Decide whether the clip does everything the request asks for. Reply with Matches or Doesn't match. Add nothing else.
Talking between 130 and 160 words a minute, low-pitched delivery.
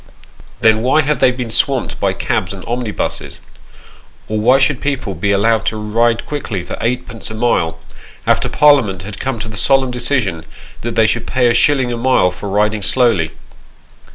Doesn't match